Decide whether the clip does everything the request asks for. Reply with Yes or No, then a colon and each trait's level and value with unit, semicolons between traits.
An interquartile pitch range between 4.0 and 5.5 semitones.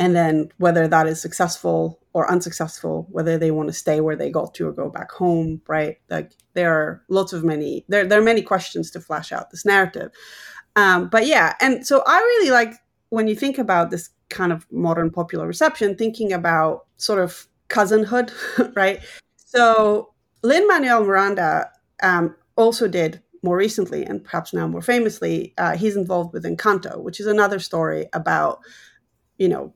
Yes: average, 4.8 semitones